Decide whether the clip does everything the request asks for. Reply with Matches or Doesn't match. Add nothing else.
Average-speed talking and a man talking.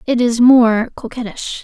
Doesn't match